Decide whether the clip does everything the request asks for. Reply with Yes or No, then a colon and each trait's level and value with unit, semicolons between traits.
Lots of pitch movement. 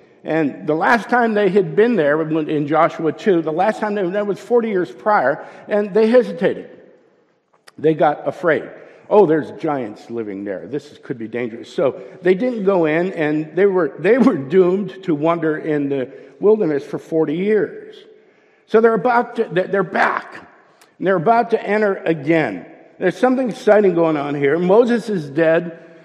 Yes: wide, 5.8 semitones